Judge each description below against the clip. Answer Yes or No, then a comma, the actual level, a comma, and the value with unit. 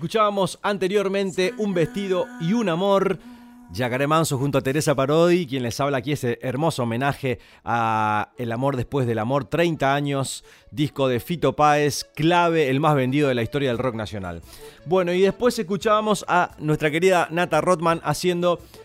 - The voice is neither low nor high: Yes, medium, 150 Hz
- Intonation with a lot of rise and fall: Yes, wide, 5.7 semitones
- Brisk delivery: No, average, 165 wpm